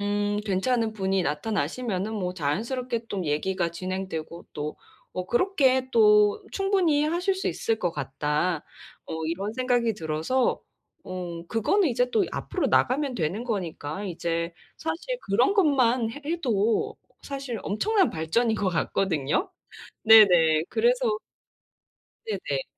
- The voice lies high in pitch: Yes, high, 210 Hz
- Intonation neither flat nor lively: No, wide, 6.9 semitones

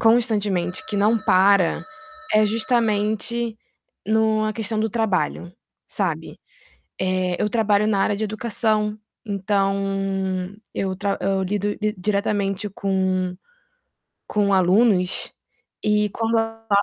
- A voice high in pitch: Yes, high, 210 Hz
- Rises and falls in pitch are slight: Yes, narrow, 2.1 semitones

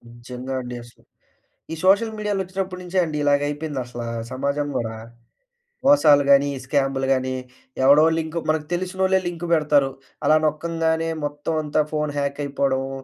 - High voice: No, medium, 145 Hz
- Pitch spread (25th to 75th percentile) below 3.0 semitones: No, average, 3.6 semitones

